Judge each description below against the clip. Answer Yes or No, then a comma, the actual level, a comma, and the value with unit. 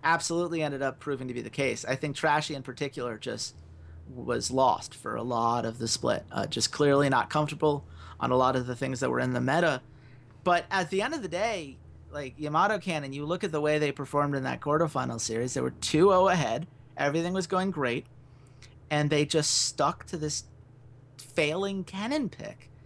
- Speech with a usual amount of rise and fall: Yes, average, 3.6 semitones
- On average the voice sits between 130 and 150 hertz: Yes, medium, 140 Hz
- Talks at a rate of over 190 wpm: Yes, average, 200 wpm